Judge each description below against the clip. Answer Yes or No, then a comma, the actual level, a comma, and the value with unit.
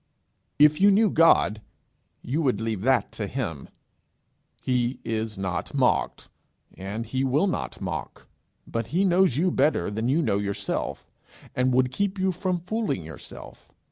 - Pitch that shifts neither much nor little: No, wide, 8.0 semitones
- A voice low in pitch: Yes, low, 130 Hz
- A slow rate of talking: No, average, 150 wpm